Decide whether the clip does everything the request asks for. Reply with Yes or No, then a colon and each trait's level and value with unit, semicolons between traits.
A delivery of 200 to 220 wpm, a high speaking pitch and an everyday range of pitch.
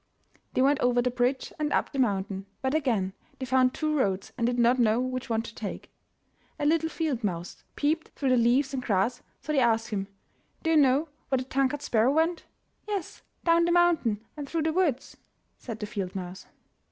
Yes: fast, 205 wpm; very high, 255 Hz; average, 4.9 semitones